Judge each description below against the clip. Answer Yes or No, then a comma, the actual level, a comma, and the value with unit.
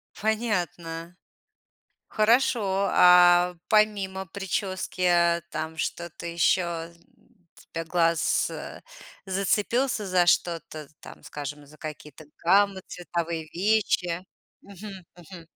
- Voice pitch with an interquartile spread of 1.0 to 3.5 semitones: Yes, average, 2.9 semitones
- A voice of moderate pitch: Yes, medium, 180 Hz